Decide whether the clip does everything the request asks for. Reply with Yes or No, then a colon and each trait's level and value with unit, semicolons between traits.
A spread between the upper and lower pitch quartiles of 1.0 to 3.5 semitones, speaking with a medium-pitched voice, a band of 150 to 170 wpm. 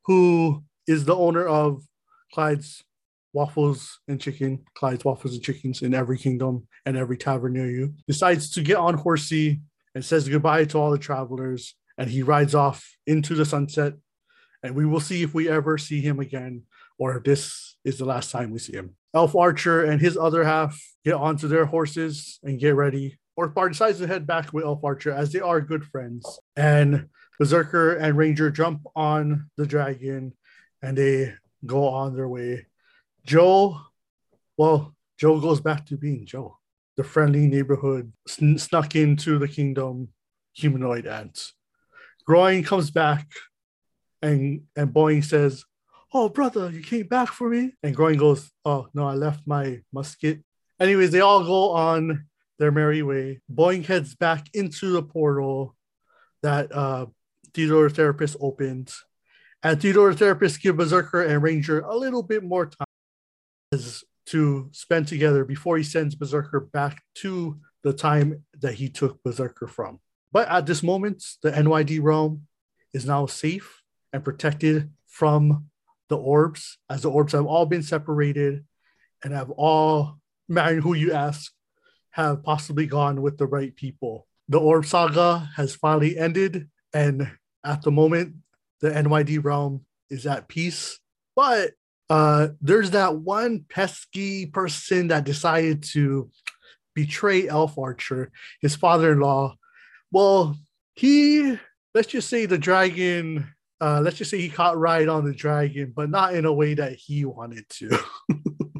Yes: average, 2.9 semitones; medium, 150 Hz; average, 155 wpm